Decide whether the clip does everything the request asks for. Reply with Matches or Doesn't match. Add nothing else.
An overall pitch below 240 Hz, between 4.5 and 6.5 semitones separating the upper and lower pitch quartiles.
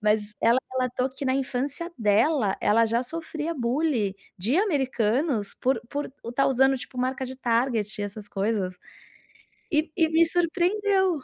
Doesn't match